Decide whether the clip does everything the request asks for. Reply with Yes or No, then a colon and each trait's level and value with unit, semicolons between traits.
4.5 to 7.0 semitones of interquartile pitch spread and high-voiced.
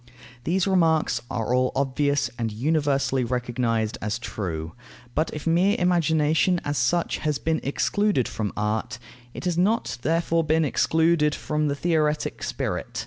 No: average, 5.1 semitones; medium, 150 Hz